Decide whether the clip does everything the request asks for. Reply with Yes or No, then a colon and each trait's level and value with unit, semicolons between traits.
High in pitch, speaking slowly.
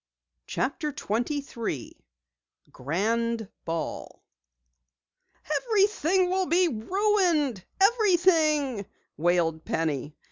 Yes: very high, 280 Hz; slow, 65 wpm